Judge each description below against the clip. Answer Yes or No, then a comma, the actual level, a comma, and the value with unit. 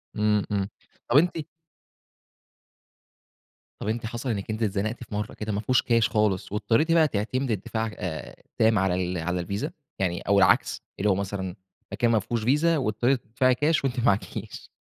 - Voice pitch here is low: Yes, low, 110 Hz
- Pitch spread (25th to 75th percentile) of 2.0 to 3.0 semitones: No, average, 3.5 semitones